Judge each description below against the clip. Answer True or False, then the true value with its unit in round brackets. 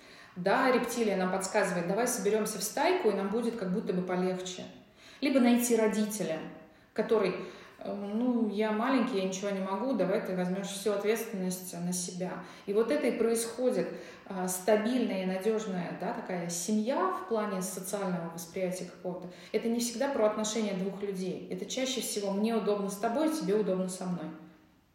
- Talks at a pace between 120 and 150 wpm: False (160 wpm)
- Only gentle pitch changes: False (3.4 semitones)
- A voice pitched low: False (200 Hz)